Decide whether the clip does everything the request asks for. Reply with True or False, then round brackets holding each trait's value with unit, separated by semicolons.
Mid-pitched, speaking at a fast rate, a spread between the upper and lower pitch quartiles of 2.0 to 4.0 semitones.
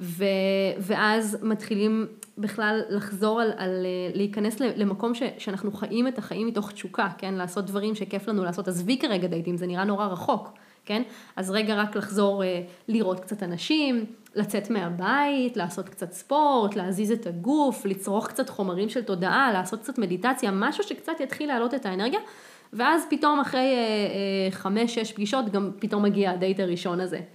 False (210 Hz; 160 wpm; 3.4 semitones)